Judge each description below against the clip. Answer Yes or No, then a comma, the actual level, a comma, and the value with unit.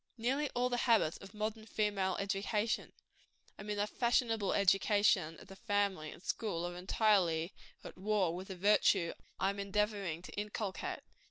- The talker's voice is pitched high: Yes, high, 205 Hz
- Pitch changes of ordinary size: No, narrow, 2.3 semitones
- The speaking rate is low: No, average, 160 wpm